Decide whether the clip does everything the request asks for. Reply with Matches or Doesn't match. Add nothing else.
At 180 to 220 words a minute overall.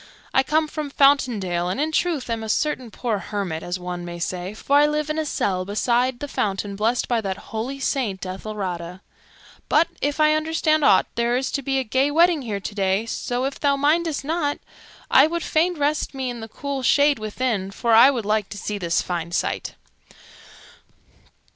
Matches